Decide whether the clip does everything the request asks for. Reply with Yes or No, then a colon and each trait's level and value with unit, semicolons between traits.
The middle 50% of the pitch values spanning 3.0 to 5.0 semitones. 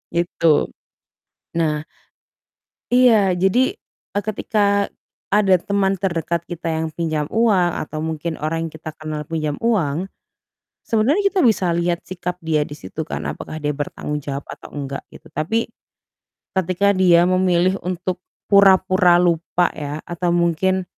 Yes: average, 3.4 semitones